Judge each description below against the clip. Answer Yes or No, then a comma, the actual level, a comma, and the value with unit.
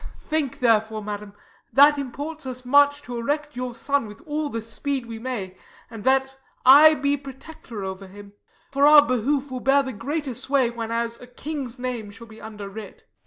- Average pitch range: Yes, average, 4.1 semitones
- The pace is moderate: Yes, average, 180 wpm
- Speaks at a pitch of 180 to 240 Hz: No, very high, 255 Hz